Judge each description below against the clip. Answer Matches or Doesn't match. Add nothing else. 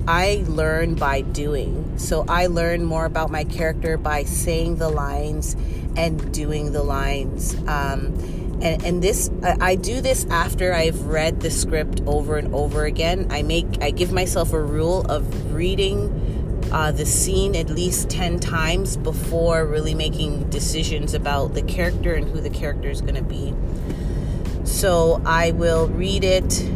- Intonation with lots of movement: Doesn't match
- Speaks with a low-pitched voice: Doesn't match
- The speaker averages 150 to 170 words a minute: Matches